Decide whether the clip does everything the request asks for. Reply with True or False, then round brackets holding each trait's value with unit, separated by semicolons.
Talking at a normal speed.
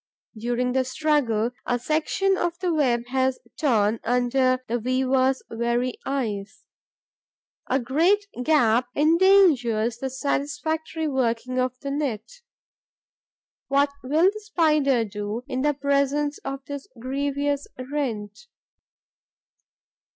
False (110 wpm)